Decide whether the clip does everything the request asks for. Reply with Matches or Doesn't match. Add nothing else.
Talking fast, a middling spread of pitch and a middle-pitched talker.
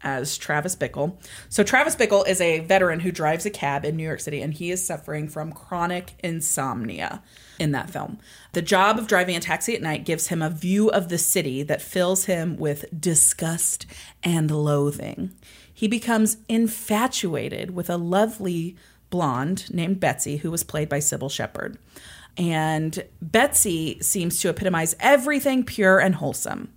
Doesn't match